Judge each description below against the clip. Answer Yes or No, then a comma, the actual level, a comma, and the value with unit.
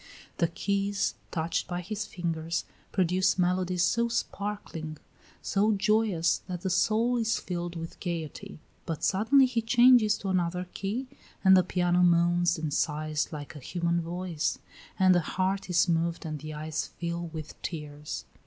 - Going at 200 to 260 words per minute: No, average, 155 wpm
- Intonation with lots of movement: No, average, 3.2 semitones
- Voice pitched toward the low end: No, medium, 180 Hz